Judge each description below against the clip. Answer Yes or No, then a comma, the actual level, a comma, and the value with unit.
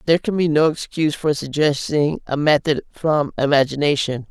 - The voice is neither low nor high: Yes, medium, 150 Hz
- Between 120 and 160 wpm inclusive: Yes, average, 155 wpm